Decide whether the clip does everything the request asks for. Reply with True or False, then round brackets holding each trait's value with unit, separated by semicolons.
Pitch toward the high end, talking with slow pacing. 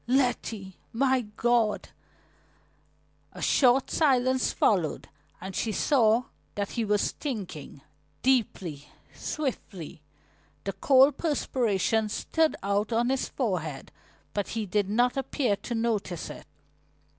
True (225 Hz; 110 wpm)